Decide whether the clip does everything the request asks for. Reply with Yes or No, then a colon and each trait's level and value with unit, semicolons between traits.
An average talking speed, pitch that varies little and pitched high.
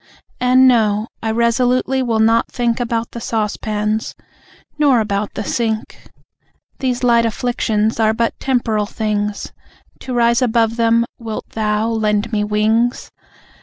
No: slow, 130 wpm; narrow, 1.9 semitones; high, 230 Hz